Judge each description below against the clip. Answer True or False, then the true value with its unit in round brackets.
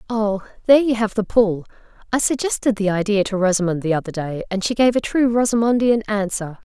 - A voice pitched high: True (210 Hz)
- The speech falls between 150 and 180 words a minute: False (190 wpm)